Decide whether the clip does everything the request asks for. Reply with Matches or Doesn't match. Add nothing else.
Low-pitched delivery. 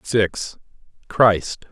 Matches